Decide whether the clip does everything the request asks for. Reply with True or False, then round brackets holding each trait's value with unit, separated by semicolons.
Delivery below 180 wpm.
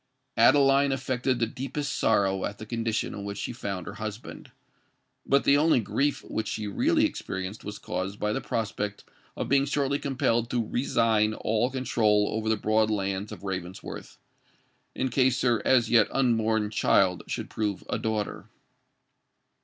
True (155 wpm)